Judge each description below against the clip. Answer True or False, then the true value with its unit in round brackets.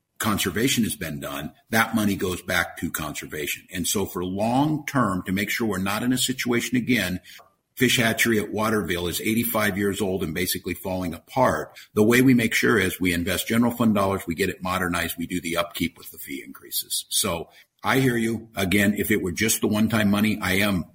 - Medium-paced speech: False (210 wpm)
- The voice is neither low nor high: False (105 Hz)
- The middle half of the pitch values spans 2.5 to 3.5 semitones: False (4.1 semitones)